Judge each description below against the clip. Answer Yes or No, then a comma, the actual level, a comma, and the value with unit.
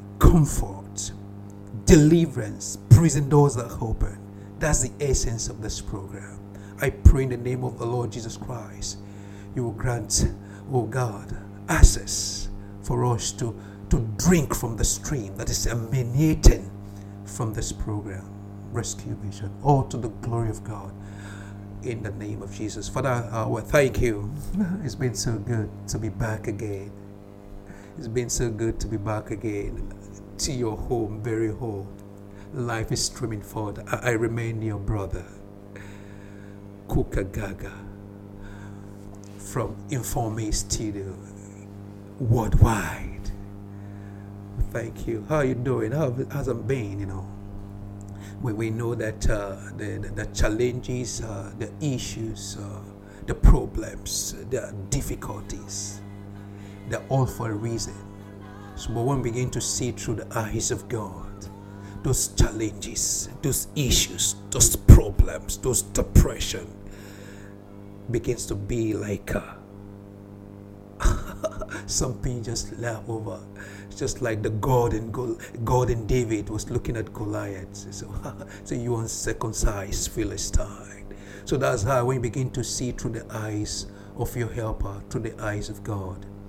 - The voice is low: Yes, low, 105 Hz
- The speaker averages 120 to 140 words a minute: Yes, slow, 135 wpm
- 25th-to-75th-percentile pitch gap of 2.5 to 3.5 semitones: Yes, average, 2.8 semitones